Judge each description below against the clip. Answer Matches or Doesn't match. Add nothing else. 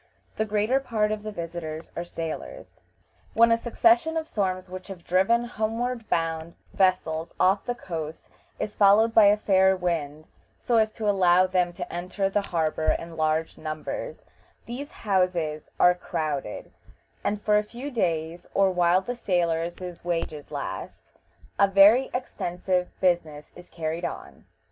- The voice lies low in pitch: Doesn't match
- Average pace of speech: Matches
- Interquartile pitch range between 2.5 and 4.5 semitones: Matches